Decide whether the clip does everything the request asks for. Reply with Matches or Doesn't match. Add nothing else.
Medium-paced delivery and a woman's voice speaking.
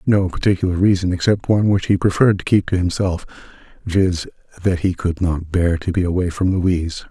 Doesn't match